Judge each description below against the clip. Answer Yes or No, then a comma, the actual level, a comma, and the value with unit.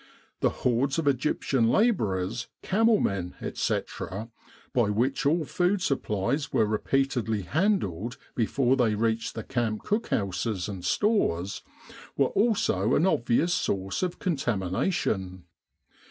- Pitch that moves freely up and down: Yes, wide, 7.8 semitones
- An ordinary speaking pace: No, slow, 115 wpm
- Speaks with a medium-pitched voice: No, low, 120 Hz